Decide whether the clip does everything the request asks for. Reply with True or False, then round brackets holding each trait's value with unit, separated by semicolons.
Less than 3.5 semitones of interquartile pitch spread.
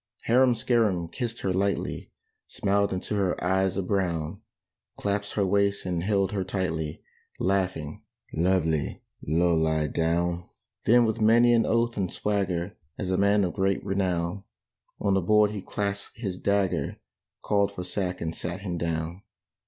True (2.7 semitones)